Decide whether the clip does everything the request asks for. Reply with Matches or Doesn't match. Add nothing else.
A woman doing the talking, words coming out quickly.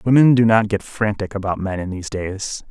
Doesn't match